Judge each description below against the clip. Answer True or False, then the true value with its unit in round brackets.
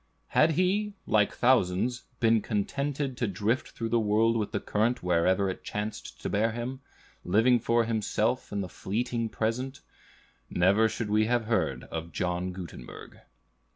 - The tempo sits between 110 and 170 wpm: True (155 wpm)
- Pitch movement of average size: True (3.5 semitones)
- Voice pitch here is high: False (110 Hz)